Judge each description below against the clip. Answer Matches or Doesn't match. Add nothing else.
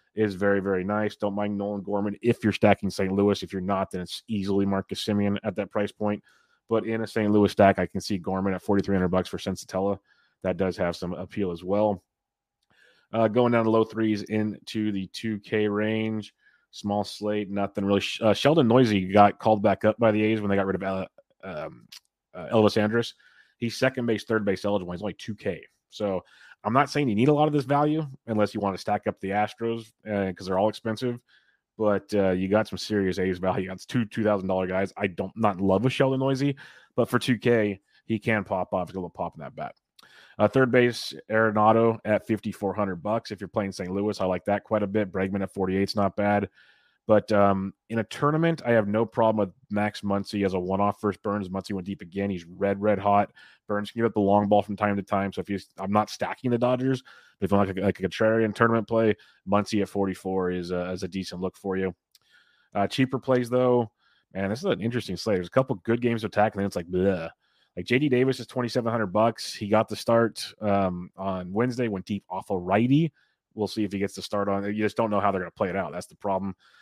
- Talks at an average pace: Doesn't match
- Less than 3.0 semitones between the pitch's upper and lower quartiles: Matches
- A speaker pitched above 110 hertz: Doesn't match